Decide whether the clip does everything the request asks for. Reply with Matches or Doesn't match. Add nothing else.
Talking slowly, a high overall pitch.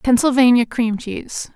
Matches